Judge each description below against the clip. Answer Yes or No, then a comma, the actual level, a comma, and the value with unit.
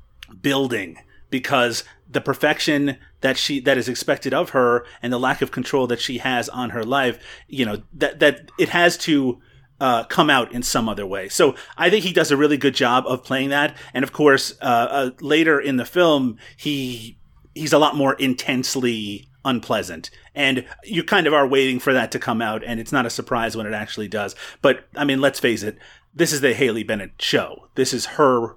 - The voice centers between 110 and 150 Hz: Yes, low, 135 Hz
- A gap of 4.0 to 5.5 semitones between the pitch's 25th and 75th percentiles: No, average, 2.9 semitones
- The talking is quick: Yes, fast, 210 wpm